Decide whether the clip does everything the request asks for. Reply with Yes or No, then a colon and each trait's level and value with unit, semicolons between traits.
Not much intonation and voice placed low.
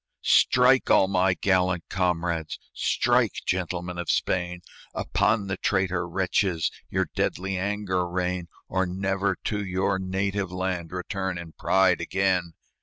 Yes: narrow, 1.4 semitones; very low, 95 Hz